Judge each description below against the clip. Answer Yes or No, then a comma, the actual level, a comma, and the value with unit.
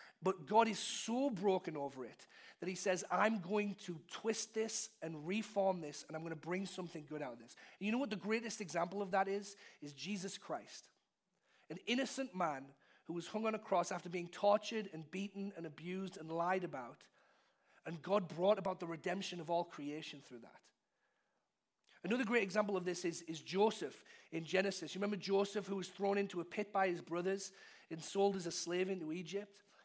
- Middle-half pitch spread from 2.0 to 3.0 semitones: No, average, 3.4 semitones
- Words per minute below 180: No, average, 200 wpm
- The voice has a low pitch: No, high, 190 Hz